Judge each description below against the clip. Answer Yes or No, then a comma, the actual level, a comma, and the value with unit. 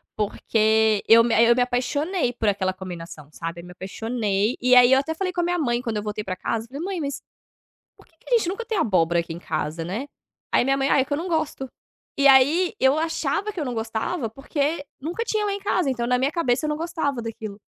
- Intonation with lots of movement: Yes, wide, 6.7 semitones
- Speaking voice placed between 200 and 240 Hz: No, very high, 250 Hz